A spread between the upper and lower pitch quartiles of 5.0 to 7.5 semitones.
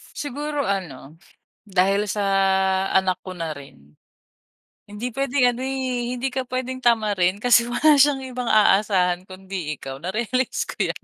Yes: wide, 5.6 semitones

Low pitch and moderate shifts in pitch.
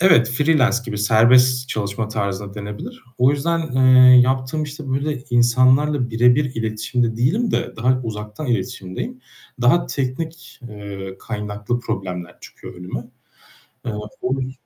Yes: low, 125 Hz; average, 3.9 semitones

